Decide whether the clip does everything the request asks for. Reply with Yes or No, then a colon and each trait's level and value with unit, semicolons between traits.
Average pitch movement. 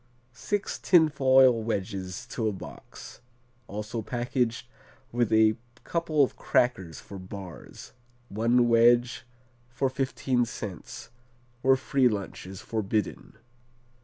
Yes: average, 3.9 semitones